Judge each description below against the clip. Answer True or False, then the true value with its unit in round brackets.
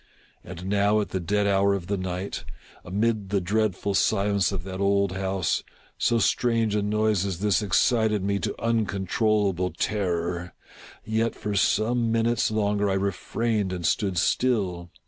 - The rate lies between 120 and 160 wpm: True (150 wpm)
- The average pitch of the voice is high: False (100 Hz)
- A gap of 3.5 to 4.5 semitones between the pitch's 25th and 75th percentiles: False (2.4 semitones)